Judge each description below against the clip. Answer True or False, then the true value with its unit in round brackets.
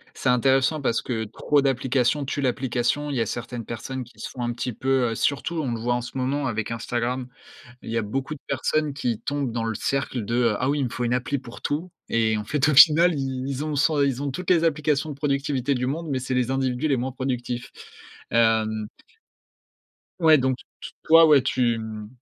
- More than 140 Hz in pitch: False (130 Hz)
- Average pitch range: True (3.0 semitones)